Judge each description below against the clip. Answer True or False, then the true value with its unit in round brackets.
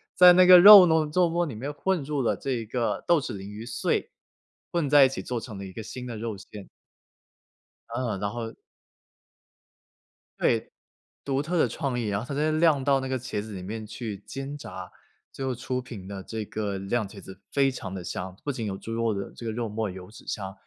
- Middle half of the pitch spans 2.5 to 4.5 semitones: False (5.3 semitones)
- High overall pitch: False (120 Hz)